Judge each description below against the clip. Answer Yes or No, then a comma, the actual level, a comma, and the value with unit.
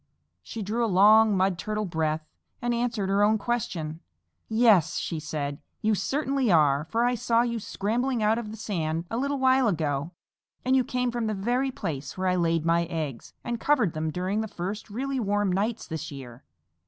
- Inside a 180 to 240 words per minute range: Yes, average, 190 wpm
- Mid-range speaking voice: No, high, 205 Hz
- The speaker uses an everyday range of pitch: No, wide, 6.2 semitones